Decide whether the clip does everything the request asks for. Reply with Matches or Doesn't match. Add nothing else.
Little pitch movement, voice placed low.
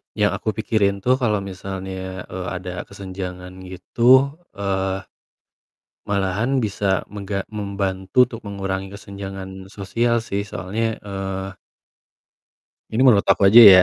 Matches